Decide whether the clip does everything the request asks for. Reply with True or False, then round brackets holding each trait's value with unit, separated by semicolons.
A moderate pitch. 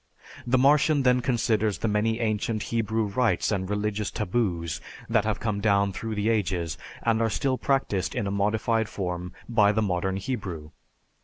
False (105 Hz)